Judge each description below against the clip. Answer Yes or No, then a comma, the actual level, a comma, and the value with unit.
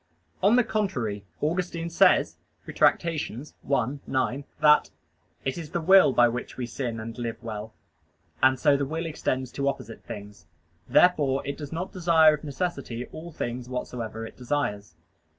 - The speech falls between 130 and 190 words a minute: Yes, average, 155 wpm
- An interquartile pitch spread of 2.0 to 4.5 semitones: No, wide, 5.4 semitones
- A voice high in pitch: No, medium, 140 Hz